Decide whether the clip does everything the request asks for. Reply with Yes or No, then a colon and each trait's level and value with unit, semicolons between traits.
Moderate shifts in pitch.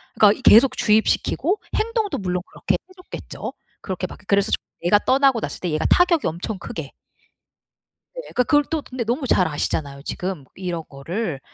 No: wide, 7.7 semitones